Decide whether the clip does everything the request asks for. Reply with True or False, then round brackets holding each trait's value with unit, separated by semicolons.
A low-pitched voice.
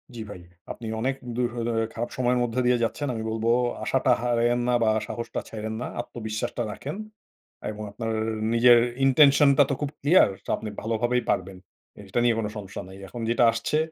True (120 Hz)